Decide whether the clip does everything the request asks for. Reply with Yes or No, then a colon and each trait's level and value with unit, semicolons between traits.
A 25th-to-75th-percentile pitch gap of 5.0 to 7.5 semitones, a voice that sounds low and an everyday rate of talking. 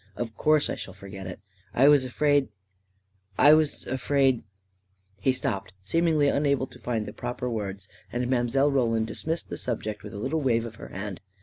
Yes: wide, 5.6 semitones; low, 120 Hz; average, 195 wpm